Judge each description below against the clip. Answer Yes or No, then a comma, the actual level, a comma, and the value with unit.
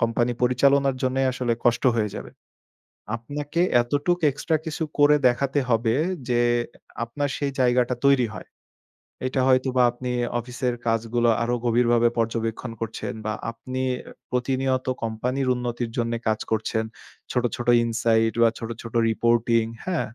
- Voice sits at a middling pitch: No, low, 120 Hz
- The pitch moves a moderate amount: No, narrow, 2.1 semitones